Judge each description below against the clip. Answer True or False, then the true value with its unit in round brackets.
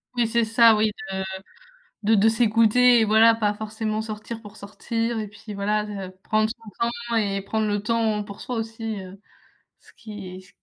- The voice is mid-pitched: False (220 Hz)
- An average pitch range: False (1.5 semitones)